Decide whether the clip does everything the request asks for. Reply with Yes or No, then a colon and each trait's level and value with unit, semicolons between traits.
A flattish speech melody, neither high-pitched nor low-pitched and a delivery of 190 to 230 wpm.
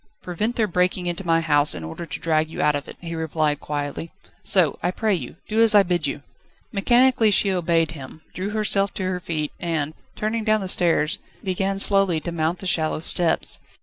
No: average, 3.9 semitones; medium, 175 Hz; fast, 205 wpm